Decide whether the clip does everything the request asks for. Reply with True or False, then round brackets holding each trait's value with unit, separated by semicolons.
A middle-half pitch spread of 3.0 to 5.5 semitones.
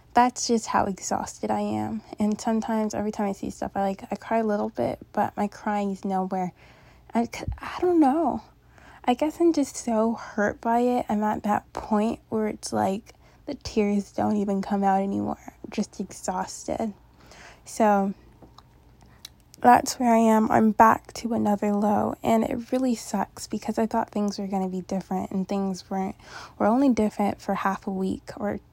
False (2.5 semitones)